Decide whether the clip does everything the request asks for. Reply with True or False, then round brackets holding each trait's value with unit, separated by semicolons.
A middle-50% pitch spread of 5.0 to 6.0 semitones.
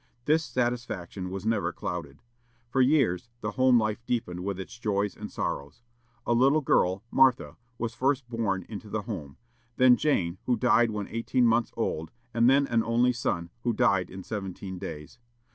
False (4.5 semitones)